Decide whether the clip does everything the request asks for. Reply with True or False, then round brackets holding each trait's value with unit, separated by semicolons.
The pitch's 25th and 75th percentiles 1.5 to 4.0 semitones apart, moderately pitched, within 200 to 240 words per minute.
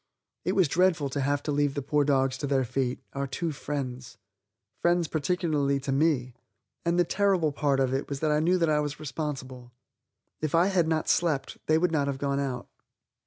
True (2.9 semitones; 145 Hz; 205 wpm)